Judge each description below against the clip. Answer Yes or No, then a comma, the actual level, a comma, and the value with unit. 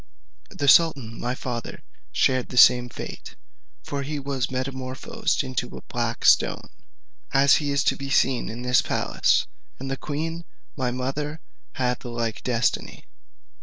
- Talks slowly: No, average, 150 wpm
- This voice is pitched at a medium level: No, low, 130 Hz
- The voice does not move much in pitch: Yes, narrow, 2.3 semitones